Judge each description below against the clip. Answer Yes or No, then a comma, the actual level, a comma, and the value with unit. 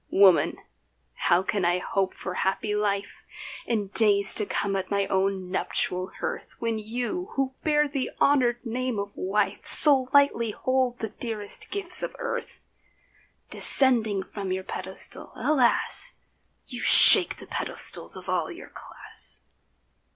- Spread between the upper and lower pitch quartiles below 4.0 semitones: No, average, 4.8 semitones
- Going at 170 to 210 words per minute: No, average, 140 wpm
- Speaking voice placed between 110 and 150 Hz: No, high, 215 Hz